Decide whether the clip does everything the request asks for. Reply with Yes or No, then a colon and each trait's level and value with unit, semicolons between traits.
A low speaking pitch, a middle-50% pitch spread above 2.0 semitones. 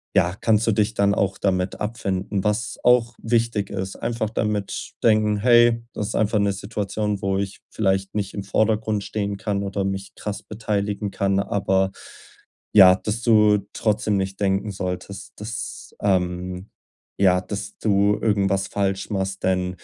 No: low, 100 Hz; narrow, 1.7 semitones